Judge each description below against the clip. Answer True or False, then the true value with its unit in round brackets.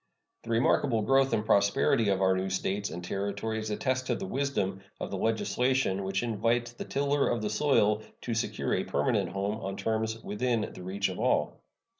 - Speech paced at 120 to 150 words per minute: False (180 wpm)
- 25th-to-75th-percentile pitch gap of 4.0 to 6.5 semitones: False (3.5 semitones)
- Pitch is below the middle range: True (110 Hz)